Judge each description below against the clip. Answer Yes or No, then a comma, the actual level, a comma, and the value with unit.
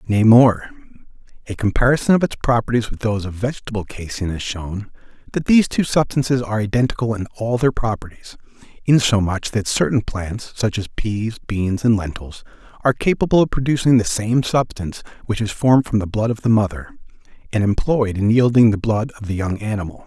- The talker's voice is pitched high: No, low, 110 Hz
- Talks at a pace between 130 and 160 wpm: No, average, 175 wpm